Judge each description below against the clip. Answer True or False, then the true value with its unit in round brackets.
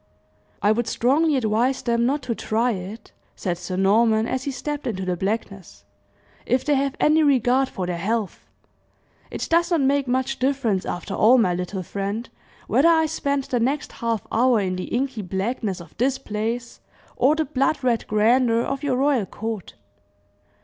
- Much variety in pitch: False (4.6 semitones)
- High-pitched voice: True (235 Hz)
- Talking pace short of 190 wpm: True (175 wpm)